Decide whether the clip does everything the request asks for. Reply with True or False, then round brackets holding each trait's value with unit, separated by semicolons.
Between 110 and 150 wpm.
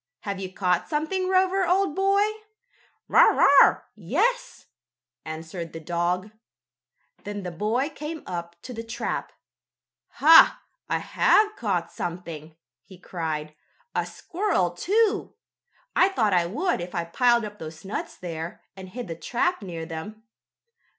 True (135 wpm)